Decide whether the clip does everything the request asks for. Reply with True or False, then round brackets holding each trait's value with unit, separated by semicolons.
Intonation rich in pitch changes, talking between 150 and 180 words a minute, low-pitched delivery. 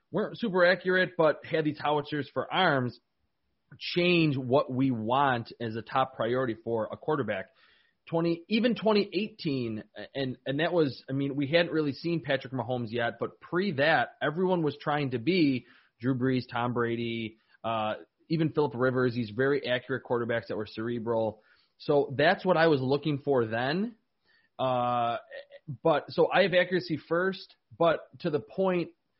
False (5.7 semitones; 160 wpm; 145 Hz)